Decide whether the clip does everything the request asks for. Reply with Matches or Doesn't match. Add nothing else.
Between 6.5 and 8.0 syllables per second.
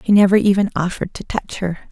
Matches